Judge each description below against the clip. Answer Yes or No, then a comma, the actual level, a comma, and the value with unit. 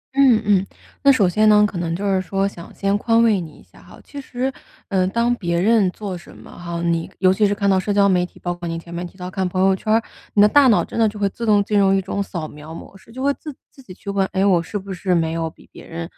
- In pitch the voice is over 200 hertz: No, high, 195 Hz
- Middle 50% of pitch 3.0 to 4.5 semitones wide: Yes, average, 3.3 semitones